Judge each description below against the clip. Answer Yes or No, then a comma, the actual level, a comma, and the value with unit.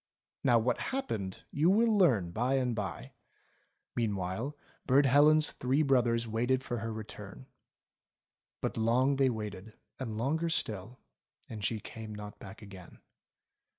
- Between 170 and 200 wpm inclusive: No, average, 140 wpm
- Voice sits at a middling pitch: No, low, 115 Hz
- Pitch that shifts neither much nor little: Yes, average, 4.3 semitones